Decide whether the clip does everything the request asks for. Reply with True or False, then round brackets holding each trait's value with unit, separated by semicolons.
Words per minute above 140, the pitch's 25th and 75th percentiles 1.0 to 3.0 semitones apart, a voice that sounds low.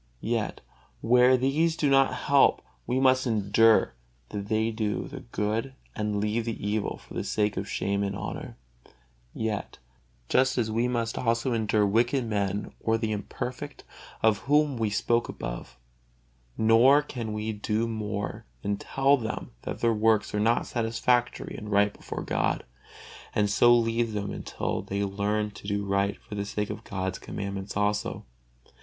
True (160 wpm; 2.7 semitones; 110 Hz)